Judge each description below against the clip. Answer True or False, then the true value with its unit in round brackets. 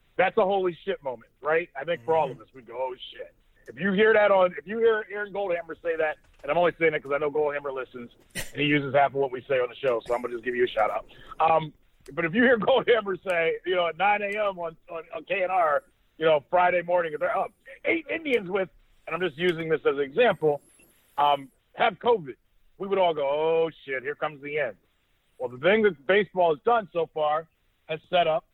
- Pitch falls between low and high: True (175 Hz)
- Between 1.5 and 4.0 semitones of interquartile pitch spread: False (5.3 semitones)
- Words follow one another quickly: True (245 wpm)